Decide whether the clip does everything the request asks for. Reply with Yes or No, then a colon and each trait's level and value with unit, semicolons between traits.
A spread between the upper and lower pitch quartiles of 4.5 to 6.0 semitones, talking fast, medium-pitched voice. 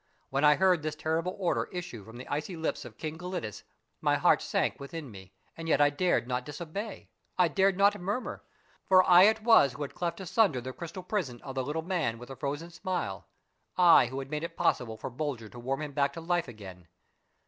Yes: wide, 5.5 semitones; fast, 215 wpm; medium, 155 Hz